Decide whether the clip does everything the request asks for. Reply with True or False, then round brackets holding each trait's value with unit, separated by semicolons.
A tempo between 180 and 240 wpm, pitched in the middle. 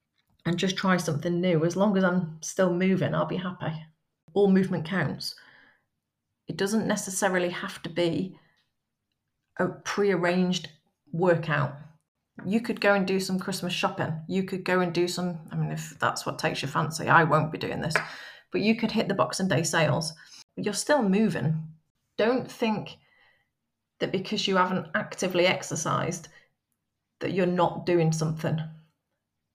False (160 wpm; 175 Hz)